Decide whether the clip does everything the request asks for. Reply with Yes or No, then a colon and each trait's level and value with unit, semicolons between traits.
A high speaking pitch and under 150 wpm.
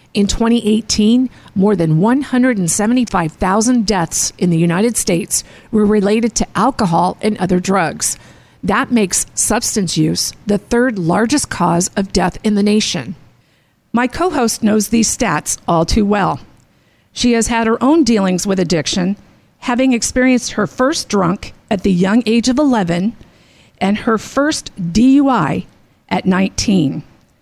Yes: high, 215 Hz; average, 140 wpm